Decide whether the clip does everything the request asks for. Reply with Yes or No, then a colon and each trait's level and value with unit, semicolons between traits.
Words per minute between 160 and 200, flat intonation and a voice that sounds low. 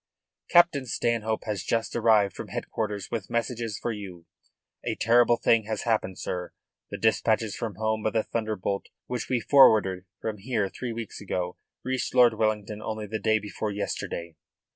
Yes: average, 165 wpm; narrow, 2.3 semitones; low, 110 Hz